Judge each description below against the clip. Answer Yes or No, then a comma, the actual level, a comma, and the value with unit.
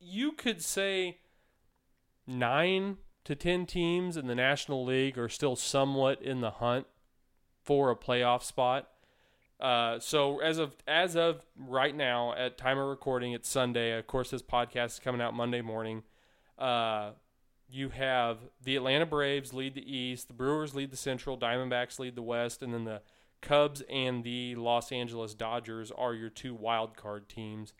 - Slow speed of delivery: No, average, 165 wpm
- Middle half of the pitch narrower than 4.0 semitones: Yes, average, 2.8 semitones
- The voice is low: Yes, low, 130 Hz